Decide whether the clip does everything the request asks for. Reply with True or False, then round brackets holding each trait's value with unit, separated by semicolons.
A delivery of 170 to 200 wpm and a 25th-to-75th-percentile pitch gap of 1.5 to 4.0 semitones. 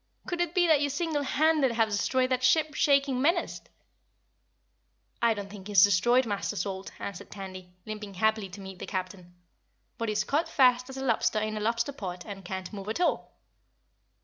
False (185 wpm; 5.4 semitones)